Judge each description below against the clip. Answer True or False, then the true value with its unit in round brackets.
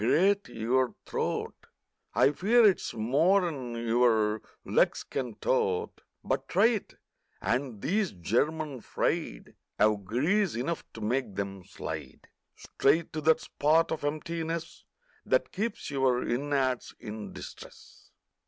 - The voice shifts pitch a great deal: True (6.4 semitones)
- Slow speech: True (120 wpm)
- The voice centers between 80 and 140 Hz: True (135 Hz)